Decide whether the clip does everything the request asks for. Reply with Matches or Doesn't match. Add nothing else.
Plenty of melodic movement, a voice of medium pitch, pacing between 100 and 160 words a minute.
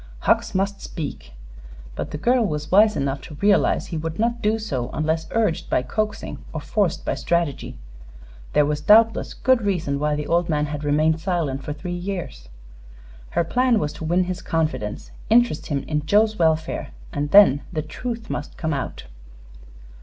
Doesn't match